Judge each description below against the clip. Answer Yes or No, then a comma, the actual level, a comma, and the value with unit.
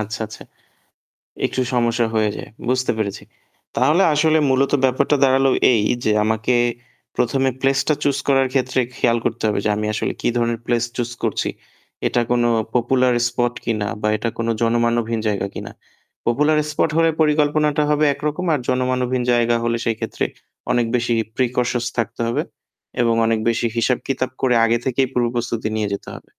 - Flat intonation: Yes, narrow, 2.3 semitones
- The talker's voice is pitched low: Yes, low, 120 Hz